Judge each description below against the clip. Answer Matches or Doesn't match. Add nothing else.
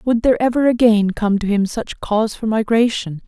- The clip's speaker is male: Doesn't match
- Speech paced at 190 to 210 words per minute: Matches